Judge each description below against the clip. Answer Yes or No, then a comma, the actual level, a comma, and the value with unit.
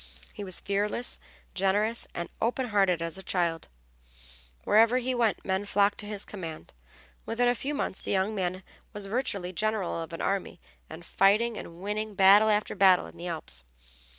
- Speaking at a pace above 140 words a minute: Yes, average, 180 wpm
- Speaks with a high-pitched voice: Yes, high, 200 Hz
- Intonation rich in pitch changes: No, average, 3.0 semitones